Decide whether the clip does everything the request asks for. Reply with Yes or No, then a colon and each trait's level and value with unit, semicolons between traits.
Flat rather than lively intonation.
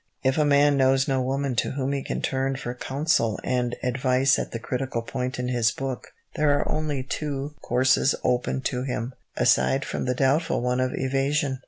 Yes: narrow, 1.7 semitones